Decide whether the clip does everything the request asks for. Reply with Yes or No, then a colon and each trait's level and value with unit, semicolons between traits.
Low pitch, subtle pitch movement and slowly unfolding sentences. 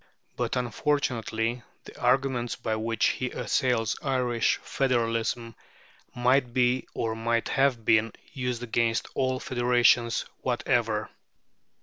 Yes: low, 120 Hz; narrow, 1.9 semitones; slow, 105 wpm